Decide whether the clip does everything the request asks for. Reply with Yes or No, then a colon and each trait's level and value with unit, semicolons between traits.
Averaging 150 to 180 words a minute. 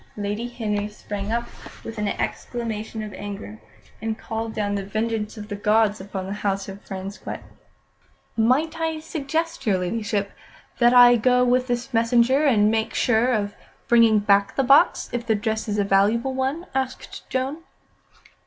Yes: average, 160 wpm